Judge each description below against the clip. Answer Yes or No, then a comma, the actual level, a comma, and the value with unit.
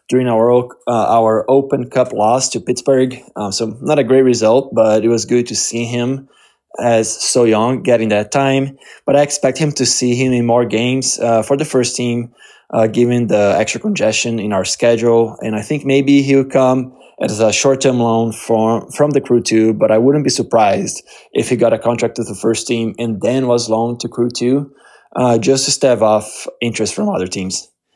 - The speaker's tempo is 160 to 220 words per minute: Yes, fast, 205 wpm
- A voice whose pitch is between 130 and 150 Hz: No, low, 120 Hz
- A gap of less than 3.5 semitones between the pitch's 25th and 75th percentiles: Yes, average, 2.7 semitones